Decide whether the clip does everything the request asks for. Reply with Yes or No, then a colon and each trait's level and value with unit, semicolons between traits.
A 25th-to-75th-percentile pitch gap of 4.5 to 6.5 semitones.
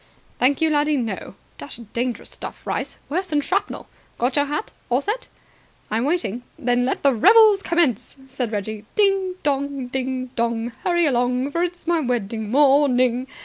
Yes: average, 4.8 semitones